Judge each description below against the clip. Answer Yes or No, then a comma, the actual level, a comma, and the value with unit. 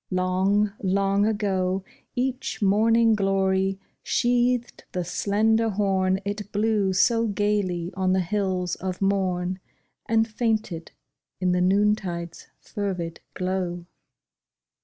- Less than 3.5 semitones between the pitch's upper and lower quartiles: Yes, narrow, 2.4 semitones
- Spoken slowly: Yes, slow, 105 wpm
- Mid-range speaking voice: No, high, 195 Hz